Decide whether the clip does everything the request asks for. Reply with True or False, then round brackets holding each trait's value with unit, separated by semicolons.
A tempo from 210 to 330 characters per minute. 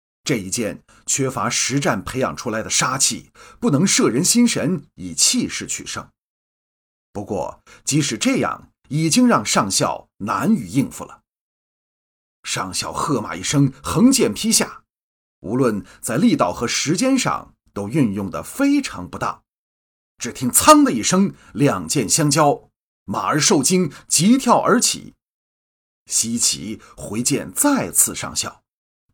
False (195 characters per minute)